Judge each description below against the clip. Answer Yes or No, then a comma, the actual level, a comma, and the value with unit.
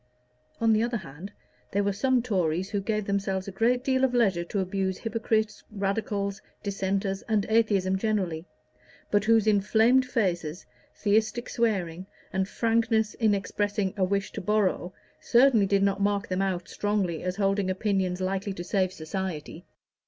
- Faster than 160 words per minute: No, average, 155 wpm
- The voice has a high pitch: Yes, high, 200 Hz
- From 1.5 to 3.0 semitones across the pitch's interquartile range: Yes, narrow, 2.6 semitones